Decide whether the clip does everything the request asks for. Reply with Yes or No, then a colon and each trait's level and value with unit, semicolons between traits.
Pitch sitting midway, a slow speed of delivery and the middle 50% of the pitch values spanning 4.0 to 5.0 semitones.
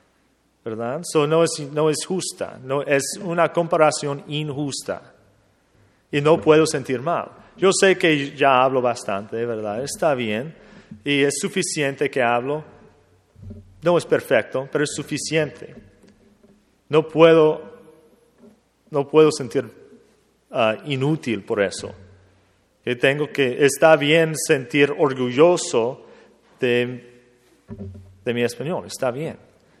Yes: medium, 145 Hz; slow, 120 wpm; average, 4.6 semitones